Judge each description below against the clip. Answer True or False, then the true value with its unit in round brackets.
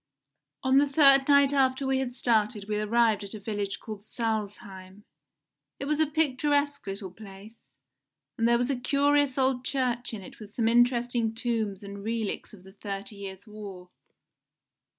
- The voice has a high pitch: True (230 Hz)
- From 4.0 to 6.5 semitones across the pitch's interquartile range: True (4.5 semitones)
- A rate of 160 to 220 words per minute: True (165 wpm)